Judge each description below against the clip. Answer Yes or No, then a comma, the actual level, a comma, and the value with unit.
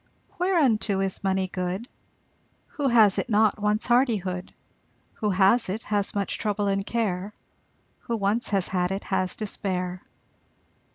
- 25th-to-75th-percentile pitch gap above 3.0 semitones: No, average, 2.7 semitones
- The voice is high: Yes, high, 200 Hz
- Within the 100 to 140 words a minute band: Yes, slow, 135 wpm